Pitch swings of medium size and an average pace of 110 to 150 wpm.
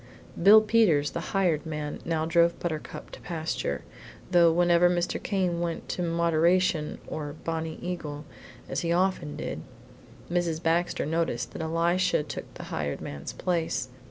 No: narrow, 2.0 semitones; average, 145 wpm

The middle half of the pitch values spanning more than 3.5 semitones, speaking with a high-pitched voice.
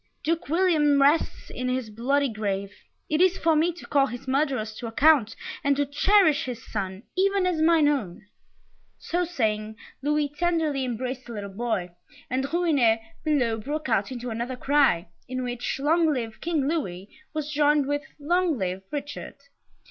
Yes: average, 5.0 semitones; very high, 275 Hz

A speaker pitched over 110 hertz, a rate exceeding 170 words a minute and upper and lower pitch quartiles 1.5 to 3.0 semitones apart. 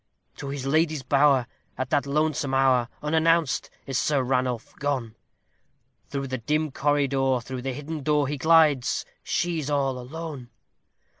No: medium, 140 Hz; average, 145 wpm; average, 2.7 semitones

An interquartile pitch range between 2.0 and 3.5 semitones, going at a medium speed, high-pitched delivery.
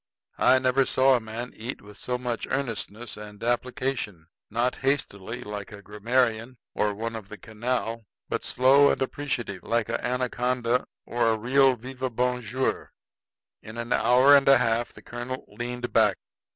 No: narrow, 2.4 semitones; average, 160 wpm; low, 120 Hz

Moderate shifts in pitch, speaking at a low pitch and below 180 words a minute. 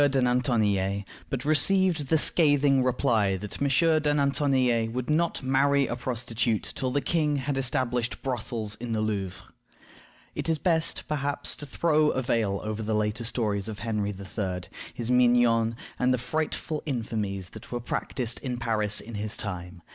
Yes: average, 4.7 semitones; low, 120 Hz; average, 160 wpm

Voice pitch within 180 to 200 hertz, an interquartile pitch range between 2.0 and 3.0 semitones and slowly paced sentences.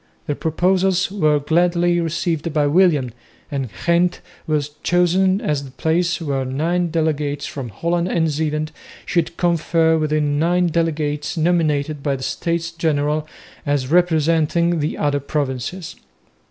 No: medium, 160 Hz; average, 2.7 semitones; slow, 130 wpm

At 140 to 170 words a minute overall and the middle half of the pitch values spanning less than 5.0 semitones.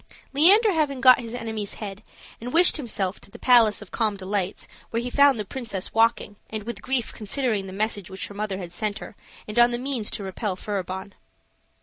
No: average, 200 wpm; average, 3.7 semitones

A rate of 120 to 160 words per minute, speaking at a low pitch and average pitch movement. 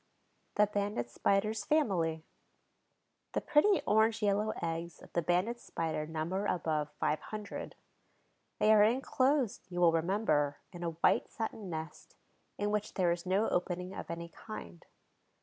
No: average, 145 wpm; medium, 185 Hz; average, 4.3 semitones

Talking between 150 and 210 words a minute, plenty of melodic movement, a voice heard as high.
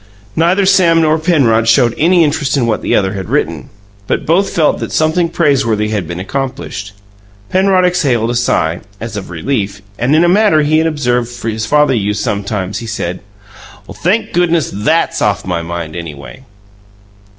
No: average, 170 wpm; wide, 8.2 semitones; low, 120 Hz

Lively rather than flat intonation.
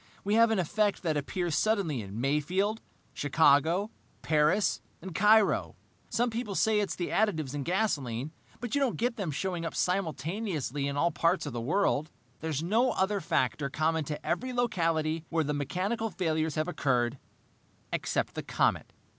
Yes: wide, 5.7 semitones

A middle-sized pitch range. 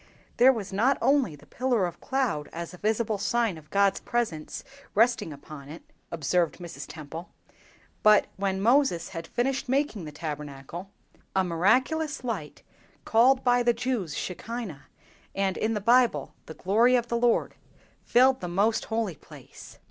No: wide, 6.3 semitones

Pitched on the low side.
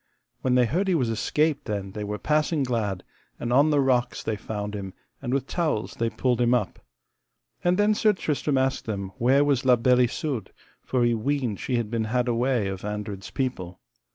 Yes: low, 125 Hz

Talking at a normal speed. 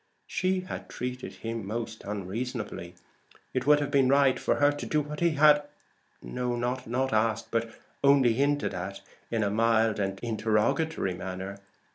Yes: average, 150 wpm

